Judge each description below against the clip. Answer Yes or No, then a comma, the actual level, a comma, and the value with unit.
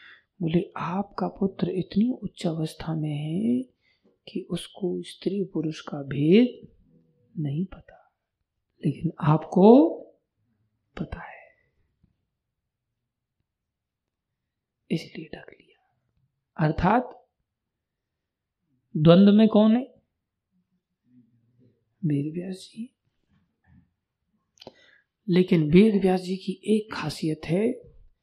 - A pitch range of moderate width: No, wide, 5.9 semitones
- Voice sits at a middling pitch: Yes, medium, 170 Hz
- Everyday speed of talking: No, slow, 85 wpm